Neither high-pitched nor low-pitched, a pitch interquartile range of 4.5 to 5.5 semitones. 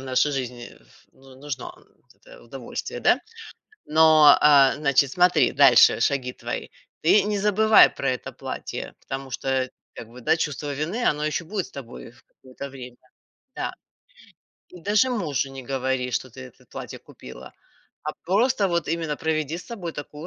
Yes: medium, 150 Hz; average, 4.8 semitones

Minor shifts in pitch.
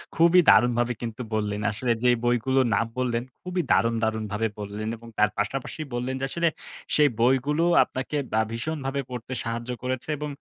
No: average, 3.0 semitones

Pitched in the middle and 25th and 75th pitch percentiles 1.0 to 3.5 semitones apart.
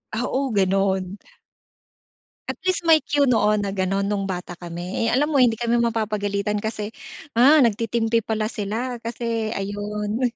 No: high, 220 Hz; average, 2.9 semitones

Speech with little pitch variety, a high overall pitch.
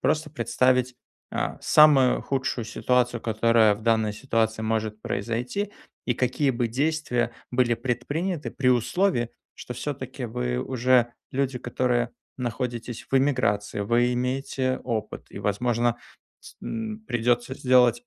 No: narrow, 2.3 semitones; low, 120 Hz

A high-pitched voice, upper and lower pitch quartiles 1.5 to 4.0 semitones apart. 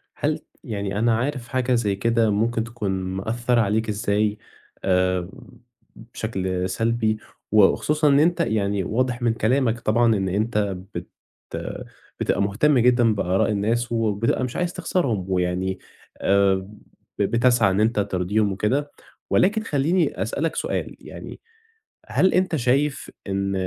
No: low, 110 Hz; average, 3.7 semitones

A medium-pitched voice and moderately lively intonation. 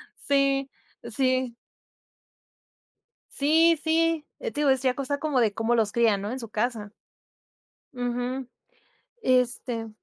No: very high, 255 Hz; average, 3.1 semitones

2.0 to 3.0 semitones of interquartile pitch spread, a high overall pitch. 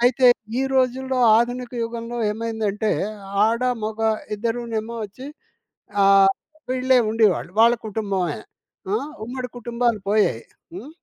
Yes: narrow, 2.5 semitones; high, 230 Hz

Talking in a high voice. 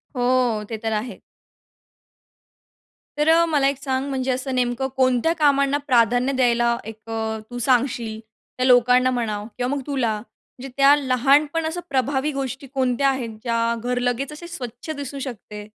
Yes: very high, 255 Hz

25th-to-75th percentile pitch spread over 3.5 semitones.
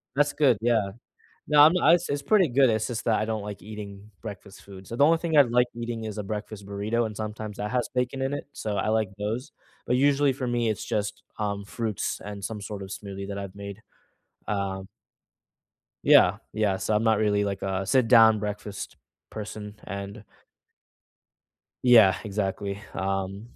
No: average, 3.1 semitones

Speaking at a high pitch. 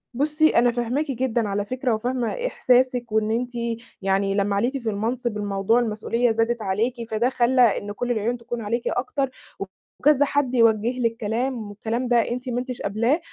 Yes: high, 235 Hz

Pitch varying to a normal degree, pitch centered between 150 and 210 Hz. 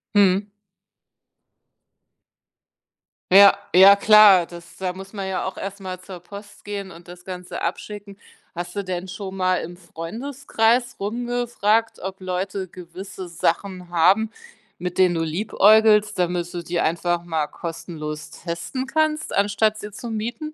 Yes: average, 3.1 semitones; high, 190 Hz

